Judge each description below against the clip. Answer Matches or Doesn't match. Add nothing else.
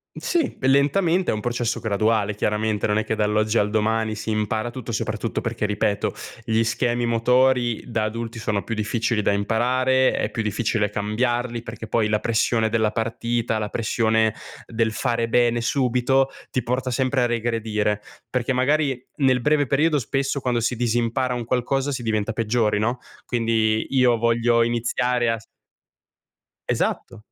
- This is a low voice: Matches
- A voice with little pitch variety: Matches